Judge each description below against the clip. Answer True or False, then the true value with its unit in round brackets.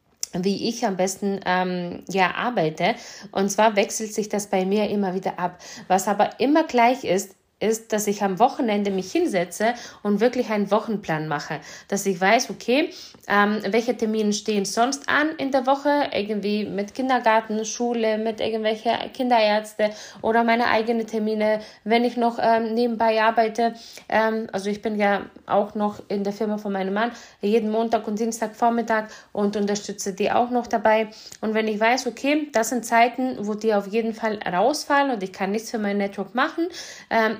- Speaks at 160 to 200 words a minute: True (180 wpm)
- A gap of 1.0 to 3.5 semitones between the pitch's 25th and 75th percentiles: True (2.5 semitones)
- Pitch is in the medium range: False (220 Hz)